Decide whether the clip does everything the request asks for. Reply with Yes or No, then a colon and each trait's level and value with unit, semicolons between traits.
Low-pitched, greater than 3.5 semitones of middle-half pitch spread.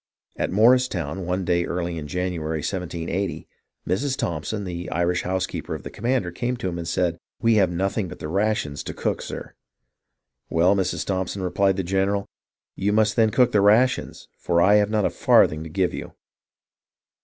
No: very low, 95 Hz; average, 3.2 semitones